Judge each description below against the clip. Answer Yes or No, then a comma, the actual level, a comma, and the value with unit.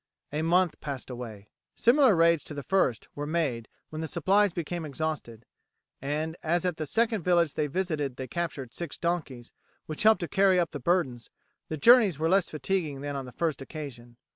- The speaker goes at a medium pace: Yes, average, 190 wpm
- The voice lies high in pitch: No, medium, 155 Hz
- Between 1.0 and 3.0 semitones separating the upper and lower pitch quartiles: No, average, 4.2 semitones